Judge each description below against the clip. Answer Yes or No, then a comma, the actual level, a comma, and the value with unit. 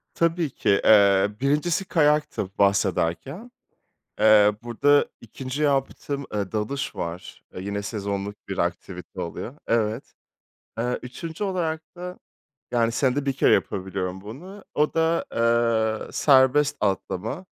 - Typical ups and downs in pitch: No, wide, 6.6 semitones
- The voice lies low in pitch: Yes, low, 115 Hz